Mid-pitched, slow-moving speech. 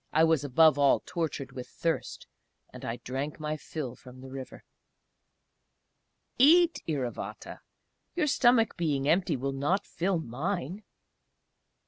Yes: medium, 155 Hz; slow, 125 wpm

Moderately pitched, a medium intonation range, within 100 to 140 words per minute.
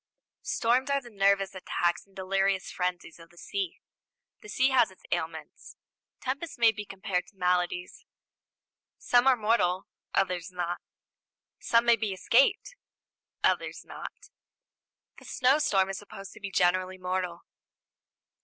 No: high, 195 Hz; average, 4.6 semitones; slow, 135 wpm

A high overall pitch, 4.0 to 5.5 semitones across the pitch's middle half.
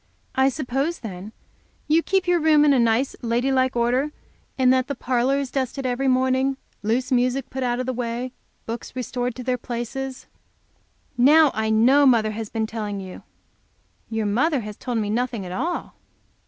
No: very high, 250 Hz; narrow, 2.6 semitones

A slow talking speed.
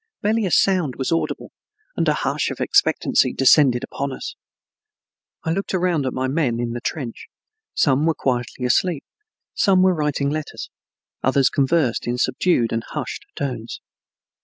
No: average, 150 wpm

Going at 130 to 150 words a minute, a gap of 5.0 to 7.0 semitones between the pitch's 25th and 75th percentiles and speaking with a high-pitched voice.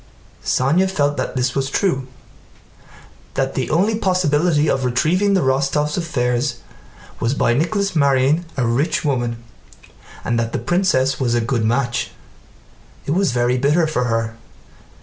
No: average, 145 wpm; average, 5.3 semitones; low, 135 Hz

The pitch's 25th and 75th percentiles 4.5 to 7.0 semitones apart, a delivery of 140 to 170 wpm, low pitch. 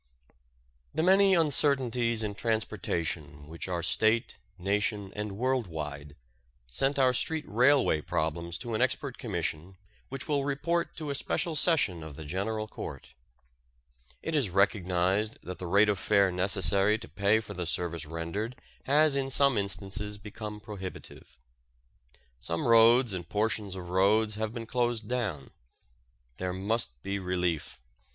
Yes: average, 5.2 semitones; average, 145 wpm; low, 105 Hz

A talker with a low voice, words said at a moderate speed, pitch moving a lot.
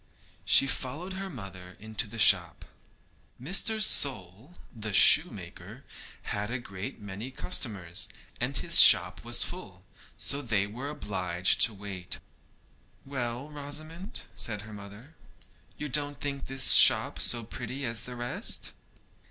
No: low, 120 Hz; slow, 130 wpm; wide, 5.7 semitones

